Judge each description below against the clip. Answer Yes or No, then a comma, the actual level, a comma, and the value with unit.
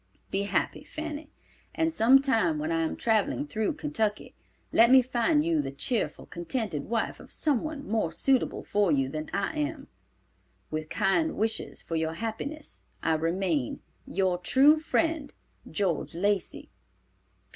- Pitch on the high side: Yes, high, 225 Hz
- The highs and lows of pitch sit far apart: Yes, wide, 9.0 semitones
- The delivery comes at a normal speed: Yes, average, 145 wpm